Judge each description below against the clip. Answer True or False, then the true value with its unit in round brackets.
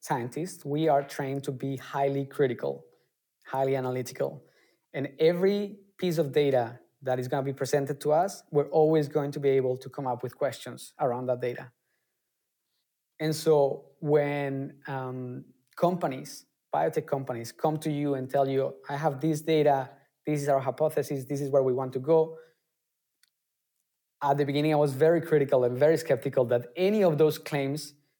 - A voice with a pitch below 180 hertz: True (140 Hz)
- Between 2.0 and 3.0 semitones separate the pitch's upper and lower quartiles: True (2.5 semitones)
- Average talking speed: True (170 wpm)